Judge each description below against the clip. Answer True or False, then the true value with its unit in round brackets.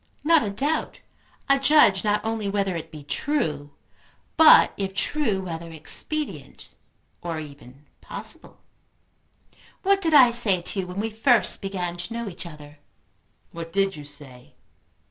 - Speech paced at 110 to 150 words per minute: True (145 wpm)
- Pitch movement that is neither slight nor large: False (6.5 semitones)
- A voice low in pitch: False (195 Hz)